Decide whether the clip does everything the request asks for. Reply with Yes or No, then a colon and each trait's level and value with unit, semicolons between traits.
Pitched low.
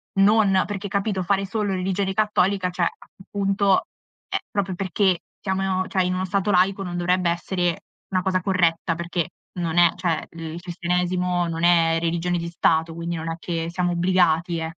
No: medium, 180 Hz